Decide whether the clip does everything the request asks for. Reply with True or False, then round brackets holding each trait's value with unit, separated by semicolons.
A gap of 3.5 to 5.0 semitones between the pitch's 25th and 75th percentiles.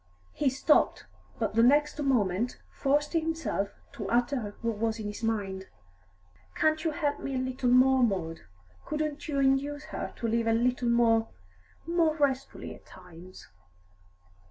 True (4.5 semitones)